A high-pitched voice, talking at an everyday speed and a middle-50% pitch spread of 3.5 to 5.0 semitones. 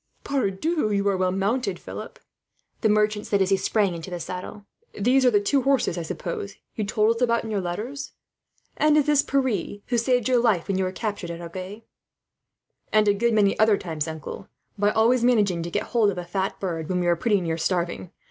No: high, 205 Hz; fast, 220 wpm; average, 4.2 semitones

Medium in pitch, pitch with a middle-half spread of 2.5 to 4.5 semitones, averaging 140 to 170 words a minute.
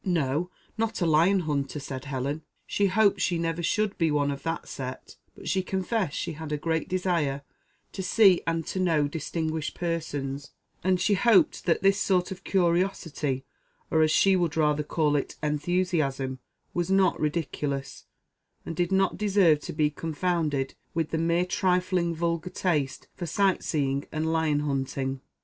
Yes: medium, 165 Hz; average, 3.7 semitones; average, 165 wpm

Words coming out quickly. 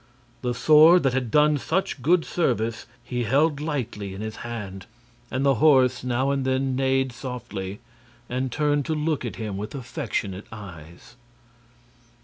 No: average, 150 wpm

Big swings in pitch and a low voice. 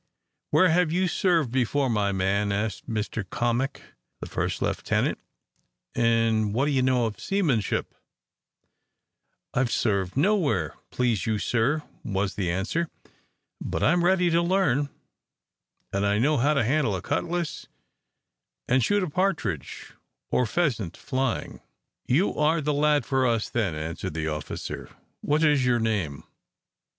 Yes: wide, 6.5 semitones; low, 125 Hz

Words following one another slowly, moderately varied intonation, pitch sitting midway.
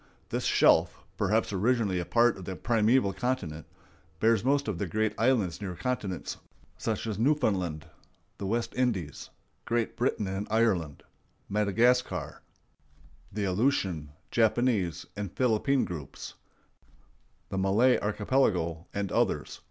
No: slow, 120 wpm; average, 4.2 semitones; low, 105 Hz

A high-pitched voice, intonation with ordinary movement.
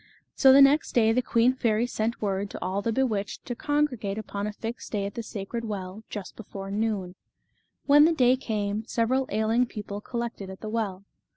Yes: high, 220 Hz; average, 3.3 semitones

